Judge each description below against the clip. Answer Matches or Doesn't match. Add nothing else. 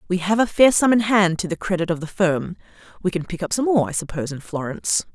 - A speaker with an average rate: Doesn't match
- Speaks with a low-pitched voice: Doesn't match